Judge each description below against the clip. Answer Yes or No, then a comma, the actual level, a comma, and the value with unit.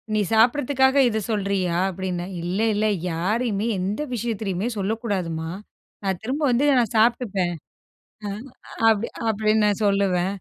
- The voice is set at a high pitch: Yes, high, 205 Hz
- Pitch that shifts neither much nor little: Yes, average, 3.3 semitones